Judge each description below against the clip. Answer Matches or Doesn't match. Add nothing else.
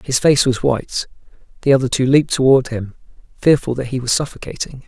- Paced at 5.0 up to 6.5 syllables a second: Matches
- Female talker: Doesn't match